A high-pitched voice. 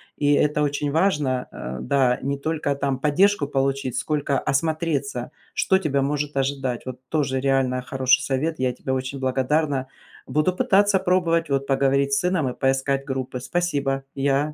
No: medium, 140 Hz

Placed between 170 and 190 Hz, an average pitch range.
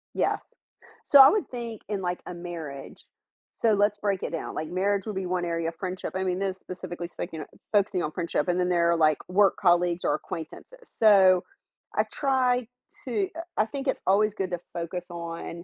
Yes: medium, 185 Hz; average, 3.3 semitones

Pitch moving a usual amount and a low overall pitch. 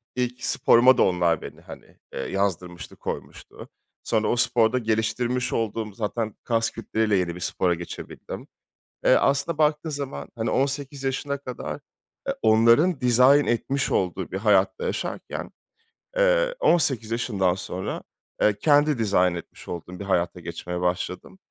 No: wide, 6.2 semitones; low, 115 Hz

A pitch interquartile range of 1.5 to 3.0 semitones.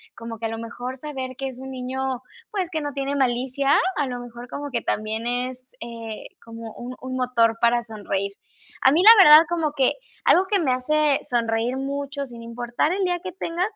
No: average, 3.6 semitones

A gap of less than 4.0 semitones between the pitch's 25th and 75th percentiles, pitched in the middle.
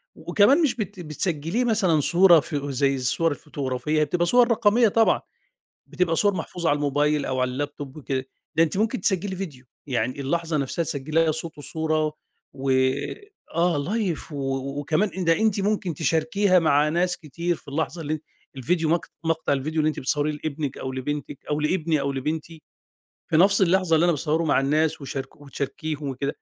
Yes: average, 3.6 semitones; medium, 155 Hz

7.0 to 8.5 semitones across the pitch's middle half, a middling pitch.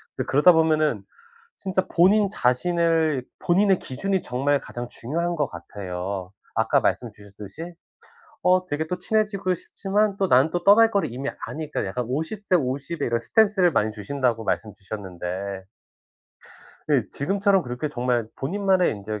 Yes: wide, 7.8 semitones; medium, 150 Hz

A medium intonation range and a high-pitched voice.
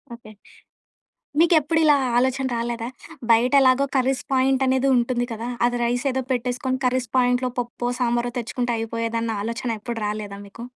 No: narrow, 1.9 semitones; high, 245 Hz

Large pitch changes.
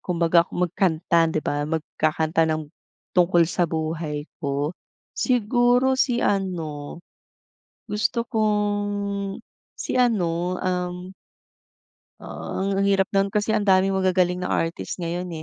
No: average, 3.5 semitones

